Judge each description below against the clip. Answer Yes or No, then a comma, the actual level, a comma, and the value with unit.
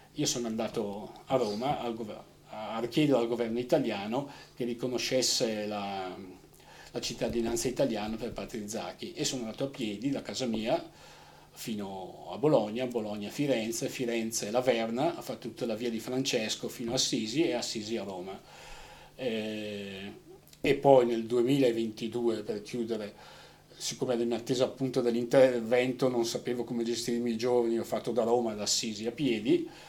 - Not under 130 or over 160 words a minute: Yes, average, 150 wpm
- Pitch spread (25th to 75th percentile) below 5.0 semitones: Yes, narrow, 2.4 semitones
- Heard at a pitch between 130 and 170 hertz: No, low, 120 Hz